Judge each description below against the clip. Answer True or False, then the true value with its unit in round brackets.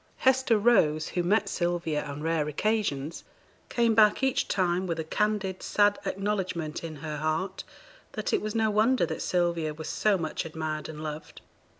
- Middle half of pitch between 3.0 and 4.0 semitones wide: False (5.1 semitones)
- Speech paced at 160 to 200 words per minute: True (170 wpm)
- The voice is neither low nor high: True (175 Hz)